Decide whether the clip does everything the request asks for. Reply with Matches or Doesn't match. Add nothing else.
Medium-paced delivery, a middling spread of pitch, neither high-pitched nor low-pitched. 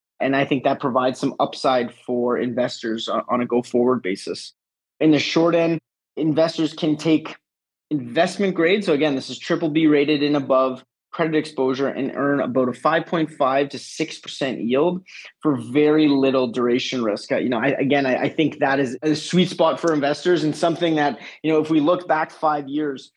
Matches